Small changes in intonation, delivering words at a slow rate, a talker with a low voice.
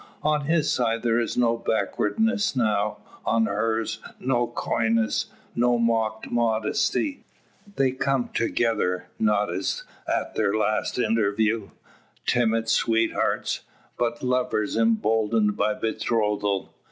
Yes: narrow, 2.1 semitones; slow, 110 wpm; low, 115 Hz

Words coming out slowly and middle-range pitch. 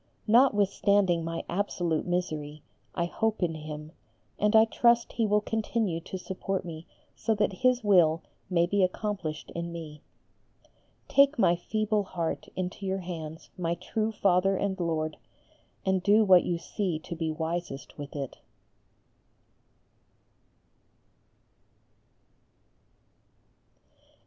Yes: slow, 120 wpm; medium, 180 Hz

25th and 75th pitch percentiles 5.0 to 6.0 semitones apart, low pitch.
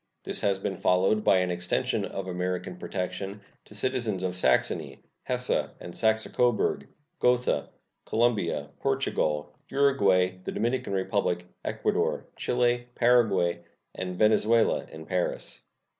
No: average, 4.3 semitones; very low, 95 Hz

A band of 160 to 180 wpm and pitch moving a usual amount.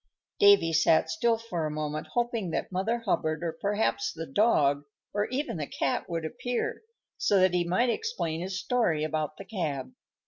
No: average, 175 wpm; wide, 6.4 semitones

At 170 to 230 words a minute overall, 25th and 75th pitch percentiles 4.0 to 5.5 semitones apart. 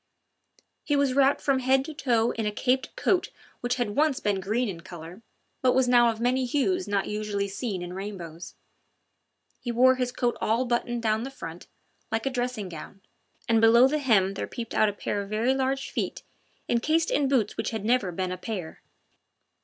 Yes: average, 195 wpm; average, 4.3 semitones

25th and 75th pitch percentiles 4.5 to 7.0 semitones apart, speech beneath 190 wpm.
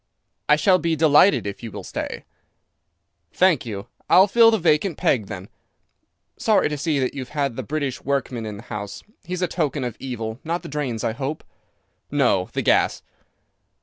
Yes: wide, 5.5 semitones; average, 180 wpm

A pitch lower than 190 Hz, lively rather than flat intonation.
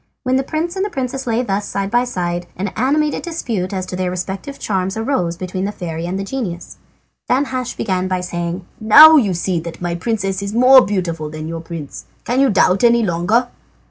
No: high, 195 Hz; wide, 5.9 semitones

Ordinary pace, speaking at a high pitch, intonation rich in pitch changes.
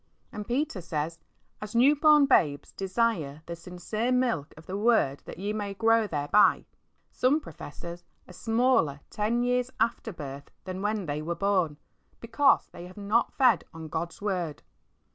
Yes: average, 160 wpm; high, 200 Hz; wide, 5.8 semitones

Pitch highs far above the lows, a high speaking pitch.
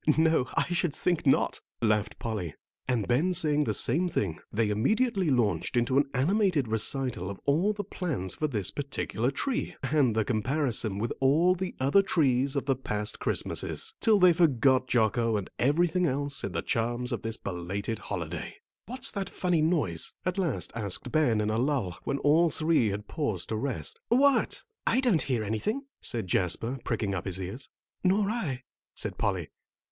No: wide, 7.4 semitones; low, 135 Hz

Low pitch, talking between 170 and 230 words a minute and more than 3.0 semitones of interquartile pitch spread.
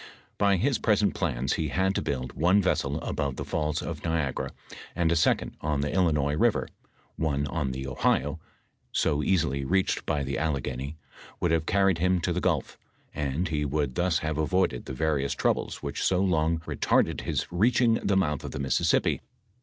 Yes: very low, 80 Hz; average, 180 wpm; average, 4.4 semitones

